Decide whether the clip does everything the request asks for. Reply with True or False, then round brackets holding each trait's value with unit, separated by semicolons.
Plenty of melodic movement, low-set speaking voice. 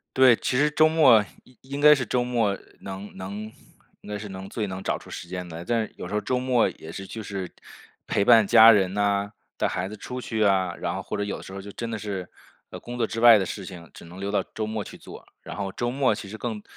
False (3.7 semitones; 105 Hz)